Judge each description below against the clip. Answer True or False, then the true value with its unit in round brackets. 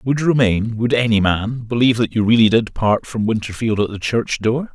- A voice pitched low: True (115 Hz)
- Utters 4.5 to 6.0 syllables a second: True (5.3 syllables/s)